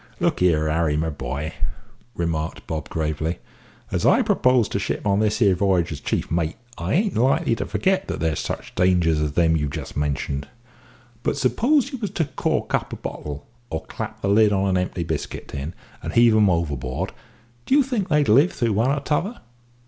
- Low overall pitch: Yes, very low, 90 Hz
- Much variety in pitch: Yes, wide, 8.4 semitones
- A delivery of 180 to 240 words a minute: Yes, average, 195 wpm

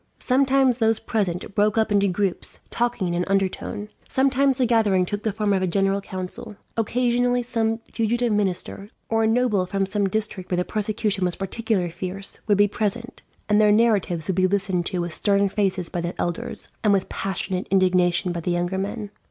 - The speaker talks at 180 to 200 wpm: Yes, average, 190 wpm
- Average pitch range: Yes, average, 3.2 semitones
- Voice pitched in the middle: No, high, 200 Hz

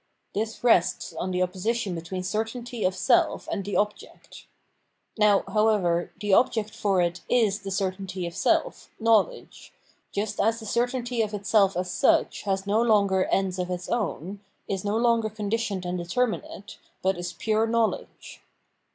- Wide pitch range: No, average, 3.2 semitones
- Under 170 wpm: Yes, average, 160 wpm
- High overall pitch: Yes, high, 205 Hz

